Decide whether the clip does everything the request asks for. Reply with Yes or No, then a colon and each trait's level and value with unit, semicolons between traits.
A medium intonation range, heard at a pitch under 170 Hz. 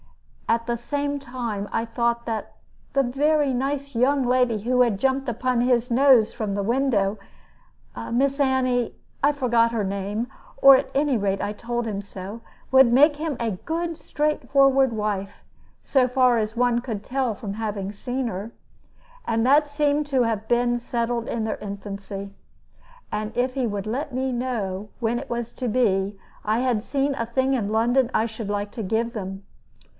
No: average, 3.7 semitones; high, 240 Hz